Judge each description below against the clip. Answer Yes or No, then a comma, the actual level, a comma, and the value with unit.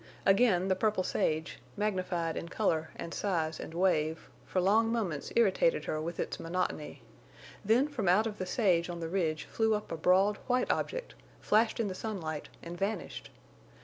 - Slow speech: No, average, 175 wpm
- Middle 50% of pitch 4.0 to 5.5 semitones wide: Yes, average, 4.4 semitones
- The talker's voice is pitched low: No, medium, 185 Hz